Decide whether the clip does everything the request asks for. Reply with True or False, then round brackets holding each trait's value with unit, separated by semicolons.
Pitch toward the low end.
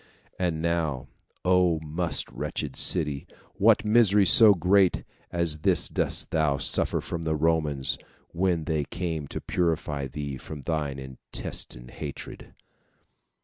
True (80 Hz)